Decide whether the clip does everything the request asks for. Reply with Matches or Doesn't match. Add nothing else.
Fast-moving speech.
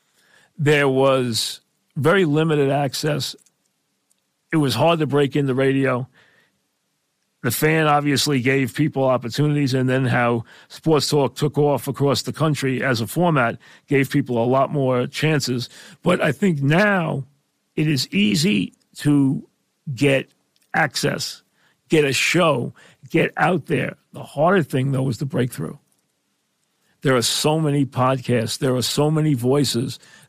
Doesn't match